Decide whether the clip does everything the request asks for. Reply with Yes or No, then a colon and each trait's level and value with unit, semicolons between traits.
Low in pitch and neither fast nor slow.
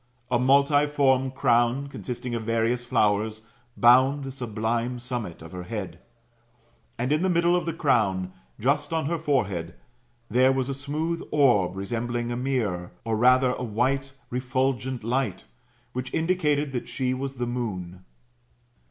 Yes: low, 125 Hz; average, 145 wpm